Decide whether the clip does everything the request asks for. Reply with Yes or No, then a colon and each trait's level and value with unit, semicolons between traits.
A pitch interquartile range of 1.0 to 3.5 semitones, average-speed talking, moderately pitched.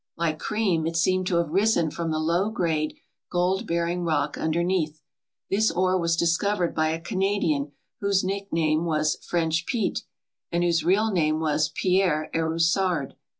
Yes: average, 2.9 semitones; average, 155 wpm; medium, 170 Hz